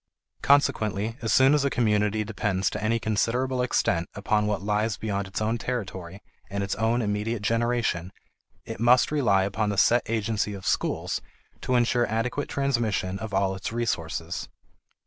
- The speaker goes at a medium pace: Yes, average, 160 wpm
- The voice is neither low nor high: No, low, 110 Hz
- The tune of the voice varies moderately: Yes, average, 3.0 semitones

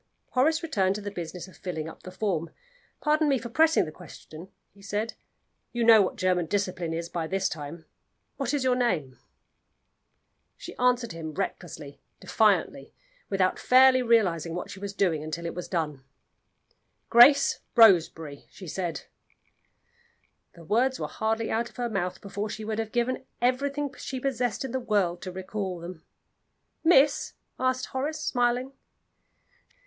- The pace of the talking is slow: No, average, 155 wpm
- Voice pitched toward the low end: No, high, 205 Hz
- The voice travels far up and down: Yes, wide, 6.2 semitones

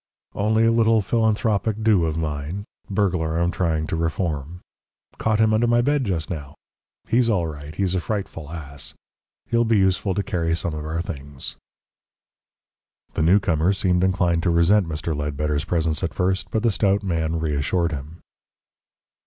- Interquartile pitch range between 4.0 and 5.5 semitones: Yes, average, 4.5 semitones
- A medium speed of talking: Yes, average, 160 wpm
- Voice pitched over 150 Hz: No, very low, 85 Hz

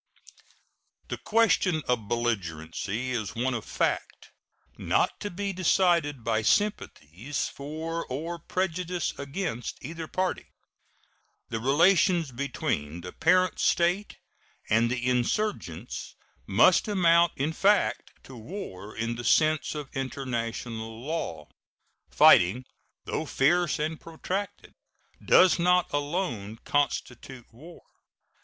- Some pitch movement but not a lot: No, wide, 6.8 semitones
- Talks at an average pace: No, slow, 110 wpm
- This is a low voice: No, medium, 145 Hz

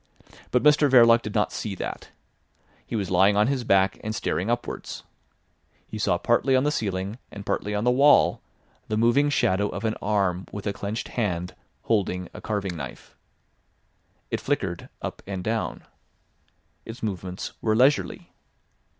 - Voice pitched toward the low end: Yes, low, 105 Hz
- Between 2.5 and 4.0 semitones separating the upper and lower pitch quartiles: Yes, average, 3.5 semitones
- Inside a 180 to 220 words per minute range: No, average, 160 wpm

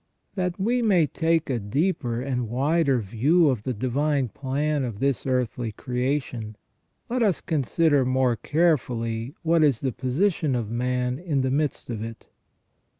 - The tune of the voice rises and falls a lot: No, average, 4.5 semitones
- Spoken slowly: No, average, 150 wpm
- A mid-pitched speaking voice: No, low, 130 Hz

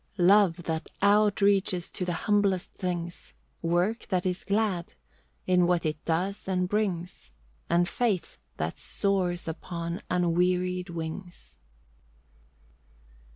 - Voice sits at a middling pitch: Yes, medium, 180 Hz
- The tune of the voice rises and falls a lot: No, narrow, 2.4 semitones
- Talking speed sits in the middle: No, slow, 110 wpm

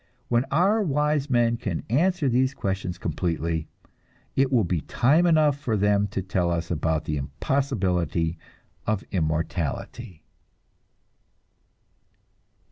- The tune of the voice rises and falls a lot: Yes, wide, 8.1 semitones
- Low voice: Yes, low, 105 Hz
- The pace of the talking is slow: Yes, slow, 115 wpm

